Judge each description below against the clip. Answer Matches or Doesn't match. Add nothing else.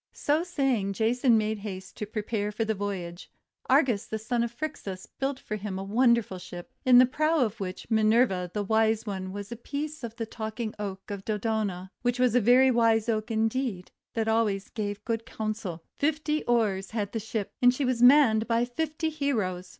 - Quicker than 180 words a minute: Matches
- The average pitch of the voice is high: Matches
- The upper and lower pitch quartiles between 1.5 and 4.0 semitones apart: Matches